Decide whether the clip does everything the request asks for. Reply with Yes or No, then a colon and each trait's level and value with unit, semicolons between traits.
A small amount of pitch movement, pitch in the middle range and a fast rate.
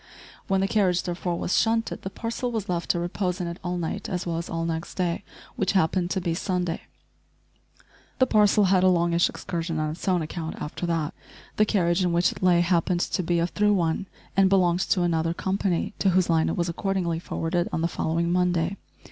Yes: narrow, 2.1 semitones; medium, 175 Hz; fast, 210 wpm